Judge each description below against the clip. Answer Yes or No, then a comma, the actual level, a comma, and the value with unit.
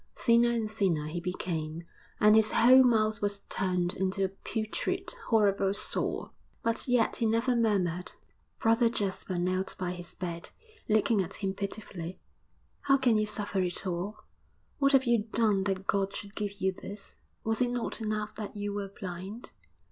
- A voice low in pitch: No, high, 205 Hz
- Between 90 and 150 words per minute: No, average, 165 wpm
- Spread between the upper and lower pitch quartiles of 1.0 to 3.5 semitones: Yes, average, 3.1 semitones